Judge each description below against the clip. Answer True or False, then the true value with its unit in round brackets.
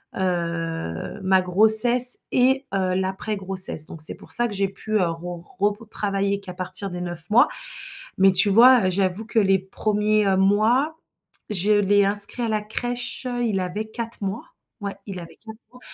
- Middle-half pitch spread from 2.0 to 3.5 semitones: True (2.8 semitones)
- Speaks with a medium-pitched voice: False (200 Hz)